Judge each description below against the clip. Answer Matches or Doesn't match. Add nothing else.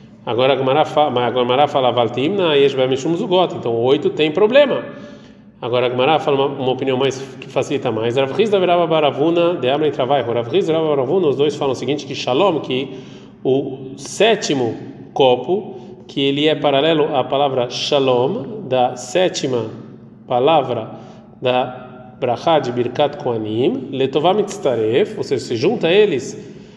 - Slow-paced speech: Matches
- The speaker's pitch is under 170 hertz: Matches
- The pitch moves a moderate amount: Matches